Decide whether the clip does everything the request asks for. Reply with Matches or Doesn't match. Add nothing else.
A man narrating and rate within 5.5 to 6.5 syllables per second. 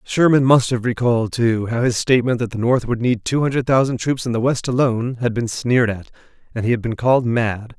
Matches